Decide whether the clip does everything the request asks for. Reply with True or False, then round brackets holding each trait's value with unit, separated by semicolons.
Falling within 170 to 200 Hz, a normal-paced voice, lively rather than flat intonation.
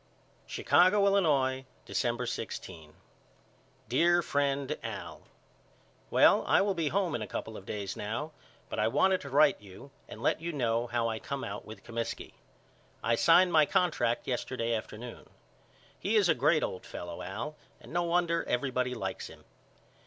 False (130 Hz; 160 wpm; 6.6 semitones)